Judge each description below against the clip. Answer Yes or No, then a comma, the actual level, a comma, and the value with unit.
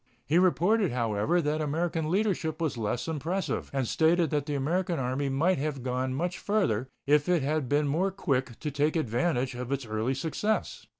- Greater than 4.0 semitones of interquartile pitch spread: Yes, average, 4.7 semitones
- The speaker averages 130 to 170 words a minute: No, average, 180 wpm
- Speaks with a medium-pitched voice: Yes, medium, 150 Hz